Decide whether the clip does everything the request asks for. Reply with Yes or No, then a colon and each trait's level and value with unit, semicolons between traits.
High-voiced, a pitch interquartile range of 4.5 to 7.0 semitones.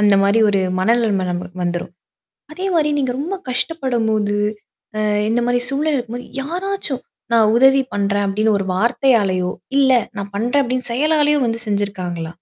Yes: high, 230 Hz; average, 5.2 semitones